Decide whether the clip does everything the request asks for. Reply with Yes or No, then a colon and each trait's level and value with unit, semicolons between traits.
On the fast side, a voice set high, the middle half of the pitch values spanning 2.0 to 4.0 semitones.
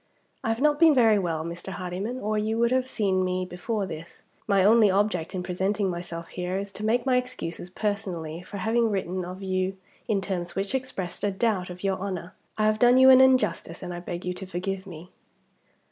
Yes: fast, 210 wpm; high, 195 Hz; average, 3.5 semitones